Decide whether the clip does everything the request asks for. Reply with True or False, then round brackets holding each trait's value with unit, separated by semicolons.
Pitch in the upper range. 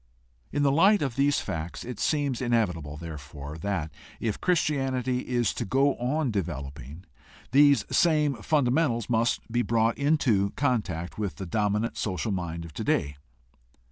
False (115 Hz)